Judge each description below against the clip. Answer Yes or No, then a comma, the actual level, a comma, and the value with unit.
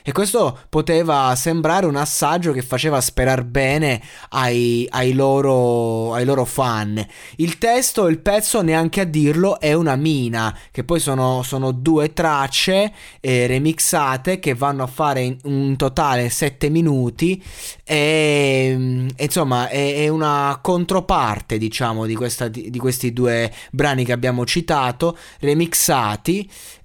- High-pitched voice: No, medium, 140 Hz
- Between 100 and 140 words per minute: Yes, average, 135 wpm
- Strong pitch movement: No, average, 4.3 semitones